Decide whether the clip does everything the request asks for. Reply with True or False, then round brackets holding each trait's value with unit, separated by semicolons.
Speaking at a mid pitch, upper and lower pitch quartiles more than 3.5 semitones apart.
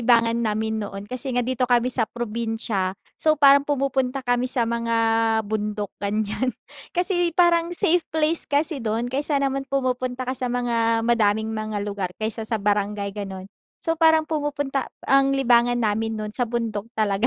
False (240 Hz; 4.0 semitones)